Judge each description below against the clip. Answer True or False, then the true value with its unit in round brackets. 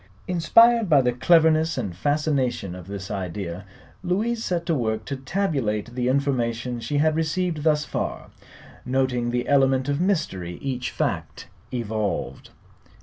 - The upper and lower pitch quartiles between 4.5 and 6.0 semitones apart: True (5.5 semitones)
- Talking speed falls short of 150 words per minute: True (140 wpm)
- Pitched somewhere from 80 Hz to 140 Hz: True (135 Hz)